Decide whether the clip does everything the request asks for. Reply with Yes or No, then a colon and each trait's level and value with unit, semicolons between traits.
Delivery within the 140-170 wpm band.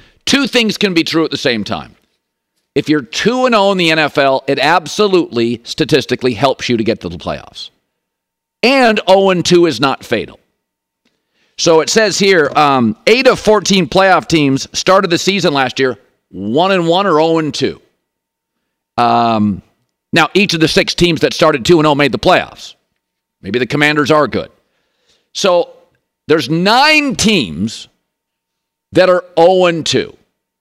Yes: average, 160 wpm